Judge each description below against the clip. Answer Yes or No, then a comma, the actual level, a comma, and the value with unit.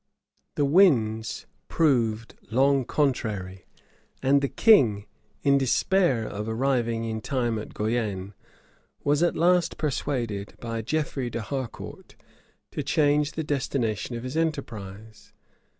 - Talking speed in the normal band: No, slow, 115 wpm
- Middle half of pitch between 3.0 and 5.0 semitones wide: Yes, average, 4.7 semitones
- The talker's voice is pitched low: Yes, low, 125 Hz